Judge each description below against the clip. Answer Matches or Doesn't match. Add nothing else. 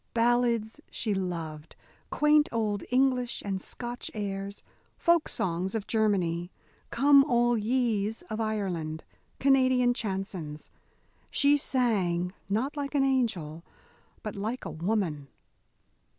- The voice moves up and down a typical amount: Matches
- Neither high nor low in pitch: Doesn't match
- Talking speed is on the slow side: Matches